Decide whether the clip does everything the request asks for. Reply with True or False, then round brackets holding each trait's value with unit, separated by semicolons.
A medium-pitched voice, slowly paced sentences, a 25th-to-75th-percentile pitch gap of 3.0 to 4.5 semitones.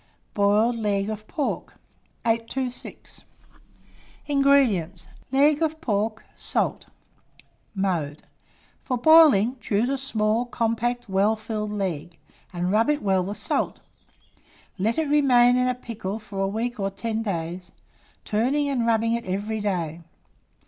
False (220 Hz; 125 wpm; 3.9 semitones)